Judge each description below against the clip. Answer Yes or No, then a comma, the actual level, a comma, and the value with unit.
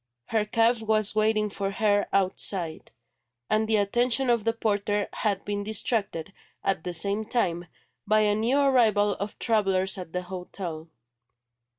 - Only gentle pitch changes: Yes, narrow, 2.3 semitones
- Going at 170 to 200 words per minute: No, average, 150 wpm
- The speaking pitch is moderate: No, high, 205 Hz